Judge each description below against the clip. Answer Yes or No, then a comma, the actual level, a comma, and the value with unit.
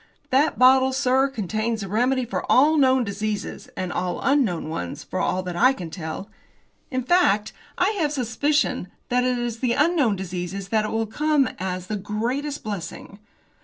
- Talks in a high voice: Yes, high, 230 Hz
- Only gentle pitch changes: No, average, 5.2 semitones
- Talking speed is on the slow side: No, average, 180 wpm